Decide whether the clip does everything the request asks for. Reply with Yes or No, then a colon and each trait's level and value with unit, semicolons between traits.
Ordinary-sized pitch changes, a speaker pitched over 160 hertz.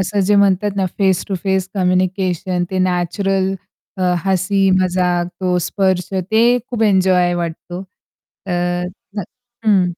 No: narrow, 1.6 semitones; medium, 185 Hz